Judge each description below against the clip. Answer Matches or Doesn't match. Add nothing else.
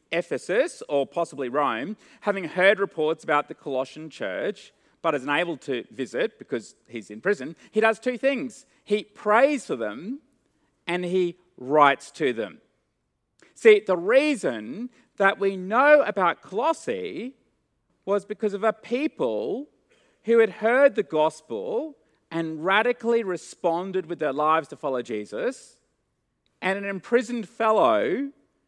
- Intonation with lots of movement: Matches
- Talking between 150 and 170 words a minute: Doesn't match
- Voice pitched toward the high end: Matches